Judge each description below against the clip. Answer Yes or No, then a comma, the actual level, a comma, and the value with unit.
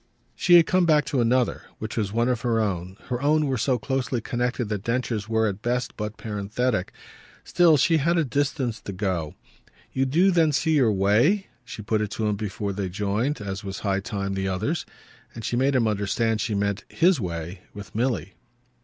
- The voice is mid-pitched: No, low, 115 Hz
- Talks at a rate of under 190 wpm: No, average, 200 wpm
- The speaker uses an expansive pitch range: No, average, 4.8 semitones